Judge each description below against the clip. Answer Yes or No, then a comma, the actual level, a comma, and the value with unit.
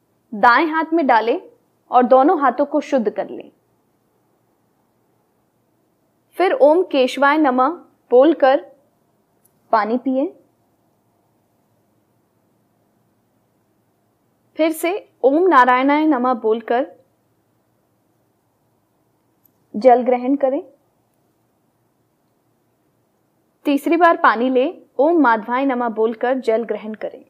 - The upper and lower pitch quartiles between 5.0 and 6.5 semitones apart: No, average, 4.4 semitones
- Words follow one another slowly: Yes, slow, 85 wpm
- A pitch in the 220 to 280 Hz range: Yes, very high, 260 Hz